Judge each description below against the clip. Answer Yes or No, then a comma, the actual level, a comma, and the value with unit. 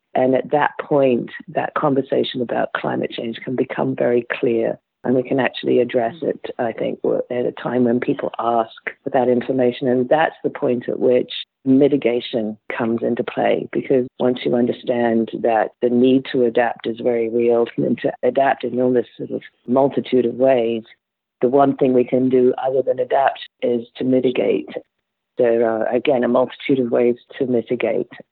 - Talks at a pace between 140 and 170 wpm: No, average, 180 wpm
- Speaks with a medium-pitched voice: No, low, 125 Hz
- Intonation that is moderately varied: No, narrow, 1.6 semitones